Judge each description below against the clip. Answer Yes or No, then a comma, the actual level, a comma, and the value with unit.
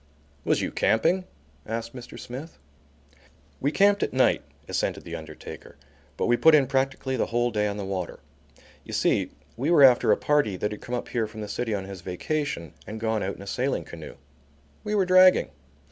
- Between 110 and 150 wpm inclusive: No, average, 195 wpm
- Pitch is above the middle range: No, low, 120 Hz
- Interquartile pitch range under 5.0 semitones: No, wide, 5.6 semitones